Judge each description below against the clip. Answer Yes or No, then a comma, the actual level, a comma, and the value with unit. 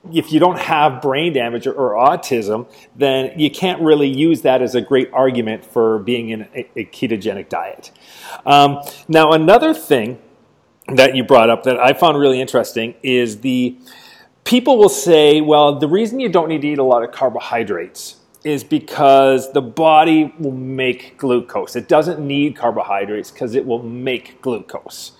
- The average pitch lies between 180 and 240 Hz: No, low, 135 Hz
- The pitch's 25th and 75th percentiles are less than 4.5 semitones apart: Yes, average, 3.9 semitones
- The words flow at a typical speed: Yes, average, 170 wpm